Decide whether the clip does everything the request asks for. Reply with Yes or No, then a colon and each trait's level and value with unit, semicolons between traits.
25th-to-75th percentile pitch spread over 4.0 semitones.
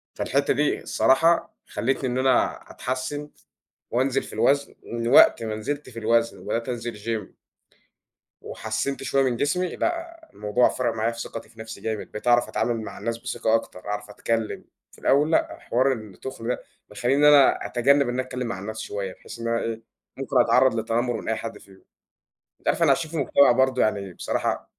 No: average, 3.3 semitones